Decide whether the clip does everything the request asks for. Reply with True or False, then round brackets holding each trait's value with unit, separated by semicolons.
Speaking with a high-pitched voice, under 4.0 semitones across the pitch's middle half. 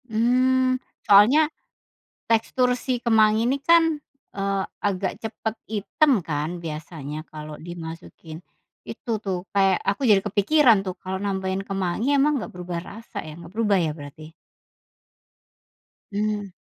False (200 Hz; 4.6 semitones)